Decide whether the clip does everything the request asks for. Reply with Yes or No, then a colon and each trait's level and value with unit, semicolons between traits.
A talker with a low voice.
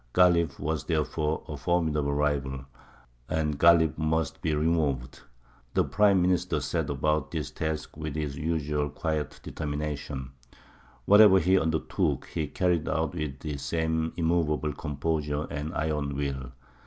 Yes: very low, 75 Hz